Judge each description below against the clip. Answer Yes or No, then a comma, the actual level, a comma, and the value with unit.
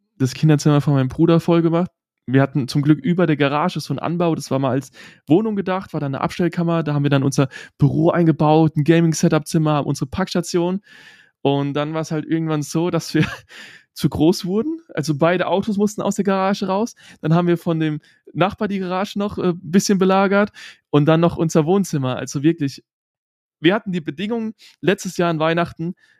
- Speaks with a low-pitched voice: No, medium, 165 Hz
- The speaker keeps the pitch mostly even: No, average, 3.7 semitones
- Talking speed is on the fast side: Yes, fast, 195 wpm